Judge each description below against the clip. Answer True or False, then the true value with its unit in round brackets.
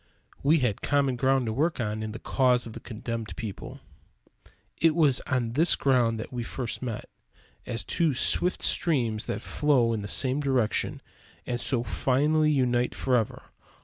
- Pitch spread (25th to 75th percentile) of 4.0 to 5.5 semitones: False (3.5 semitones)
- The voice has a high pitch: False (125 Hz)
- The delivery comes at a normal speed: True (165 wpm)